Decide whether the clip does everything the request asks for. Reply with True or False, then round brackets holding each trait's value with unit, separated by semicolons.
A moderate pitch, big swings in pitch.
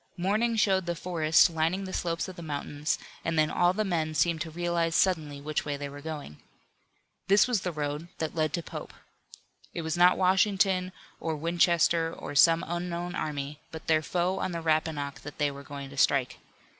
False (165 Hz; 2.8 semitones)